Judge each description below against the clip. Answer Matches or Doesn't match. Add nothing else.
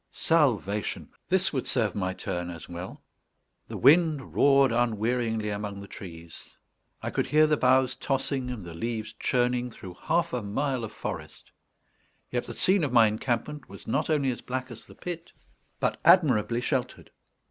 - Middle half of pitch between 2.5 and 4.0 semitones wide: Doesn't match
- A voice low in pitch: Matches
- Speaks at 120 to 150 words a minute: Doesn't match